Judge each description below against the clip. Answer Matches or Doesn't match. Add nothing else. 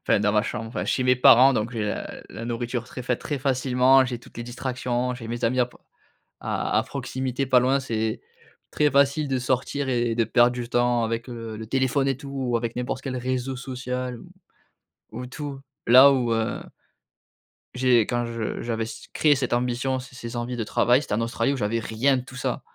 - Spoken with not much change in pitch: Matches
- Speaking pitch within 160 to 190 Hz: Doesn't match